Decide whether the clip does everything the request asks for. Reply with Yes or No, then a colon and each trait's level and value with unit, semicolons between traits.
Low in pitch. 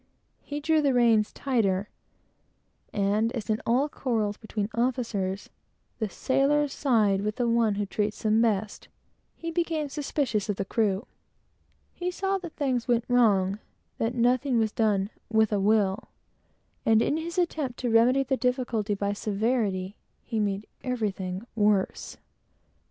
No: high, 225 Hz